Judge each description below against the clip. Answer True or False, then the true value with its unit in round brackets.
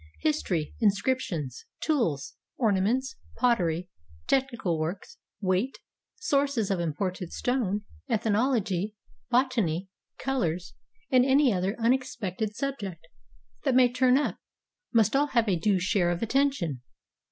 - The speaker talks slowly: True (120 wpm)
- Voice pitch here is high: True (215 Hz)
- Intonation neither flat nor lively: False (6.1 semitones)